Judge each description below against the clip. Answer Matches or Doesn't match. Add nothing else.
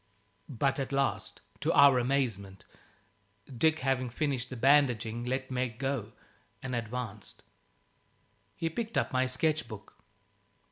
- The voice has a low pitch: Matches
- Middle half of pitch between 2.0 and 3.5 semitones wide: Matches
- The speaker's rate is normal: Doesn't match